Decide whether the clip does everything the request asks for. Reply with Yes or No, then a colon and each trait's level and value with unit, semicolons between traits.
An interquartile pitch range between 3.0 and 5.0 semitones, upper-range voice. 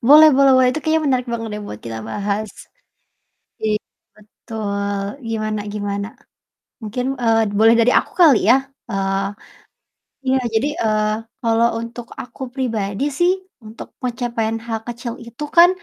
Yes: average, 3.3 semitones; high, 230 Hz